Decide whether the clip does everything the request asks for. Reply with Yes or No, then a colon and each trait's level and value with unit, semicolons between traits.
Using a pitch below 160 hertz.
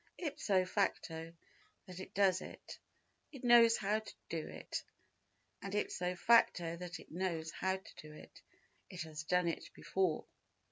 No: medium, 185 Hz